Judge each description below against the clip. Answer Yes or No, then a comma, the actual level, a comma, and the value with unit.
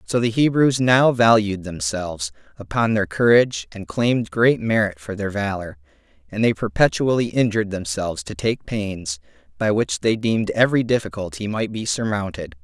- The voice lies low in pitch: Yes, low, 105 Hz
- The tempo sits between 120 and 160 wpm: Yes, average, 155 wpm